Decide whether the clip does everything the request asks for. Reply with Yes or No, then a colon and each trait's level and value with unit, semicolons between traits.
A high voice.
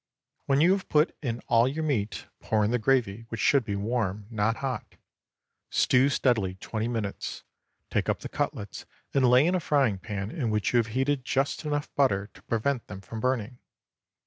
No: low, 120 Hz